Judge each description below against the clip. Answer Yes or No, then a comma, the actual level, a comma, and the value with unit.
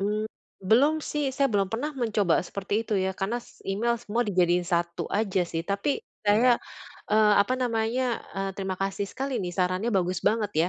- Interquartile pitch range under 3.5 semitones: No, average, 3.9 semitones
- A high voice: Yes, high, 205 Hz